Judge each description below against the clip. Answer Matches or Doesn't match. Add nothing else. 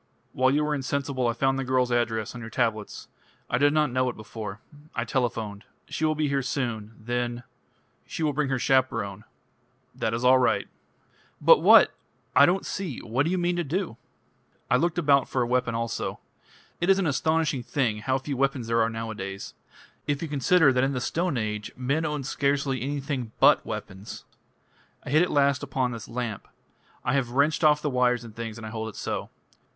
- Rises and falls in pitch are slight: Doesn't match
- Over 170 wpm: Matches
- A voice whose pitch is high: Doesn't match